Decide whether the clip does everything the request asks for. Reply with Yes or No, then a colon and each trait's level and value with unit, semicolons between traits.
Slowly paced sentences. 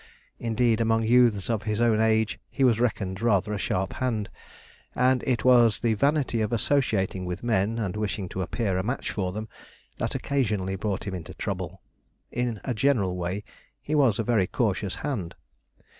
No: average, 175 wpm